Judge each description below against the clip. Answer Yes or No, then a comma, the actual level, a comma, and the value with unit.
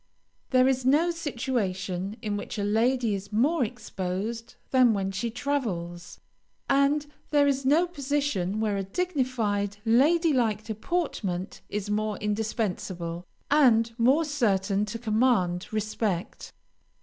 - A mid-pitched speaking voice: No, high, 225 Hz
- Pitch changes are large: No, average, 4.8 semitones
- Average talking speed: No, slow, 125 wpm